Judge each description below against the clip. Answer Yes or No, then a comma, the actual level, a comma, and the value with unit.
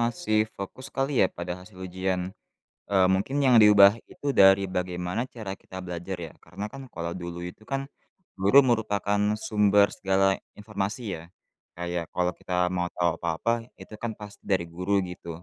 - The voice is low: Yes, very low, 95 Hz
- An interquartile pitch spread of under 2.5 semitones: No, average, 2.8 semitones